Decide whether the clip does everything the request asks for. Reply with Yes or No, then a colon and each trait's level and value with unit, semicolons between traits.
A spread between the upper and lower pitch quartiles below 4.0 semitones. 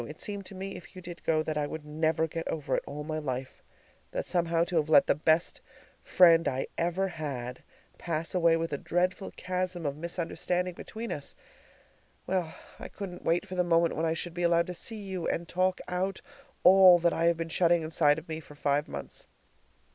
Yes: narrow, 2.4 semitones